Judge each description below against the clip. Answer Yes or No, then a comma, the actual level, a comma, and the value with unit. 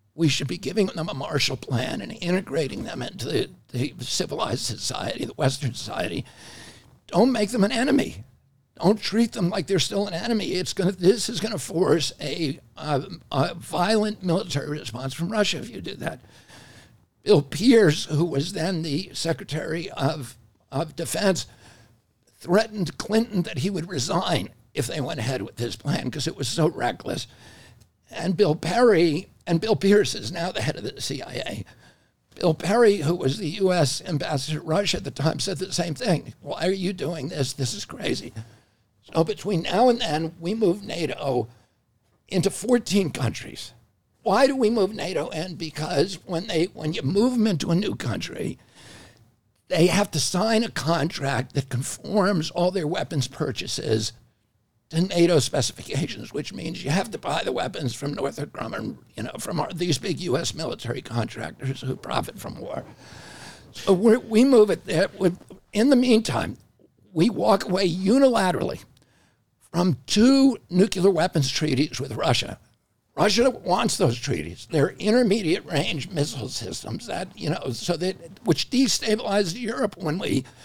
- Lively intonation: Yes, wide, 6.9 semitones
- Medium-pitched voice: Yes, medium, 165 Hz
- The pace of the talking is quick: No, average, 165 wpm